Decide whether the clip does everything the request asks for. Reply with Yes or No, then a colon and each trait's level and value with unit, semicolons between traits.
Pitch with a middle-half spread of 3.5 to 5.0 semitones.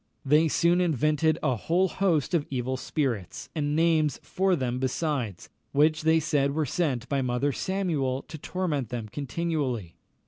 Yes: average, 4.0 semitones